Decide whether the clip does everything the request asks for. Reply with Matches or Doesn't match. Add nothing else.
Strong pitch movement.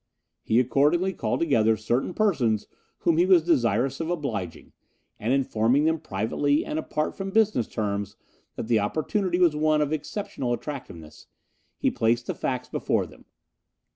Matches